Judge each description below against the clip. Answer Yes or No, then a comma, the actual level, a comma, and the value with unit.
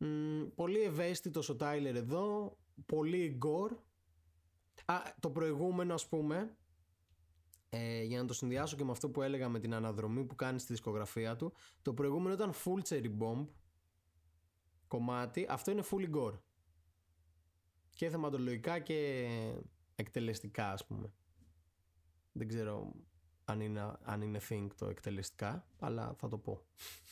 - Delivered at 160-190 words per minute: No, average, 135 wpm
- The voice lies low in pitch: Yes, low, 115 Hz